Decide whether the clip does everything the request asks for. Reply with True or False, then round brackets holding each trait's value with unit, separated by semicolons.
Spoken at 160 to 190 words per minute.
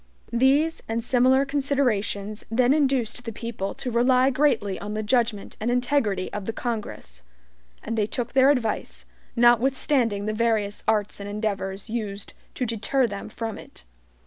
False (150 wpm)